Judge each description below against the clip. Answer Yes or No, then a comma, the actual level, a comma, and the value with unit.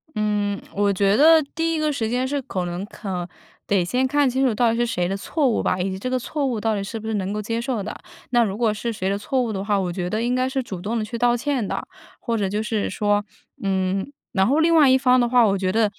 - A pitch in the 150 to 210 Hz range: No, high, 220 Hz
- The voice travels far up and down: No, average, 4.2 semitones